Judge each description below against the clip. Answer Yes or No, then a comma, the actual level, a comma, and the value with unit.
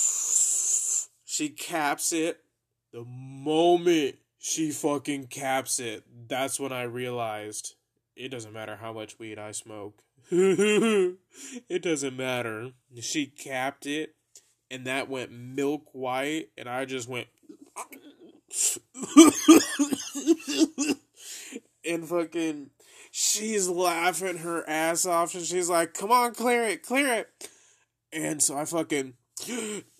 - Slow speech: Yes, slow, 110 wpm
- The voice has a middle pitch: Yes, medium, 160 Hz